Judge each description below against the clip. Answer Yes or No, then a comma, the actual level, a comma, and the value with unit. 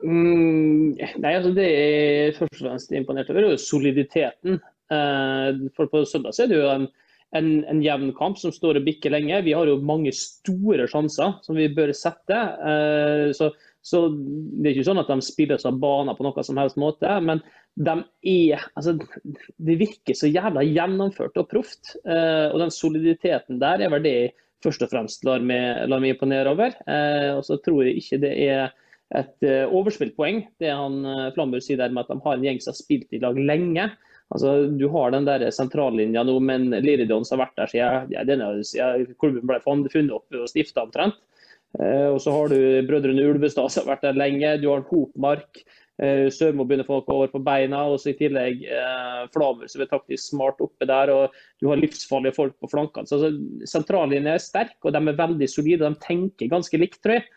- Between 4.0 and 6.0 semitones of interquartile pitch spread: No, average, 2.7 semitones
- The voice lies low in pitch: No, medium, 145 Hz